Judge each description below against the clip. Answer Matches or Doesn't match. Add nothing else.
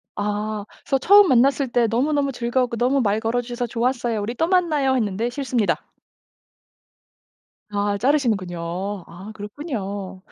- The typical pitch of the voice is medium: Doesn't match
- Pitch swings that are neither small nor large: Matches